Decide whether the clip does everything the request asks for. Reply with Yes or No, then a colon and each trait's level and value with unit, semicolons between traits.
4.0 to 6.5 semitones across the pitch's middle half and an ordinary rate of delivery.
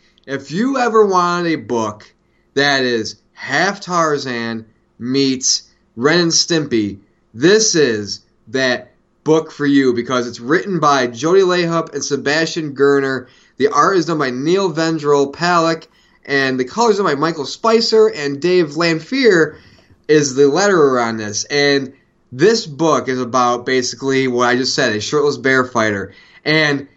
Yes: average, 4.7 semitones; average, 150 wpm